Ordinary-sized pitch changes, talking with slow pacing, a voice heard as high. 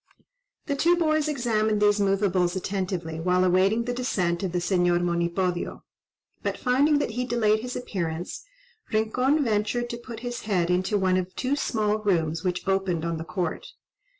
No: average, 5.0 semitones; average, 165 wpm; high, 200 Hz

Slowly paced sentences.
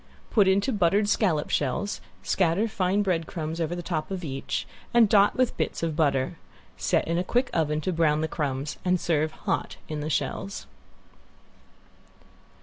No: average, 165 wpm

